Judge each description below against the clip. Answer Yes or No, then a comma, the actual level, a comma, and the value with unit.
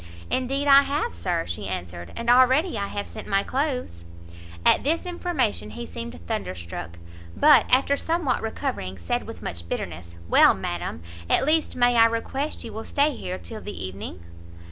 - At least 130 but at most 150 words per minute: No, average, 165 wpm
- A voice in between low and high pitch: No, high, 235 Hz